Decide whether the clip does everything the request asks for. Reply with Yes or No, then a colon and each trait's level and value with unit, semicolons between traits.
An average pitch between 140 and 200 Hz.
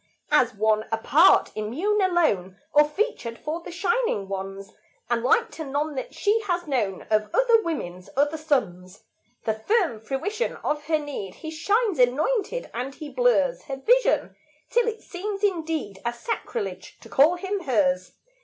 No: very high, 300 Hz